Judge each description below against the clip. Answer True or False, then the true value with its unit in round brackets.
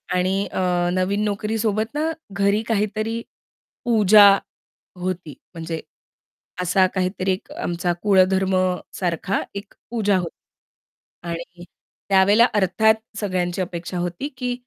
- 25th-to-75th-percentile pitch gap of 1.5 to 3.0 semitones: True (2.7 semitones)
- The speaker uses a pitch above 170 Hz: True (190 Hz)